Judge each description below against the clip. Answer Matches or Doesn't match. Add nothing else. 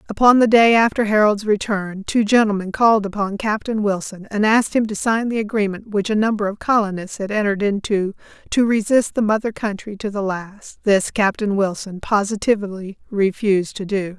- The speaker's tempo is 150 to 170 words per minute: Doesn't match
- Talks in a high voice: Matches